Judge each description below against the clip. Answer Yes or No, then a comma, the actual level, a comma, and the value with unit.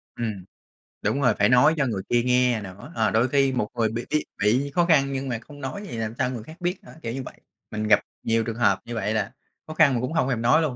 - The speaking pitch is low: Yes, low, 125 Hz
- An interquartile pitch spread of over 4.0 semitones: No, average, 3.7 semitones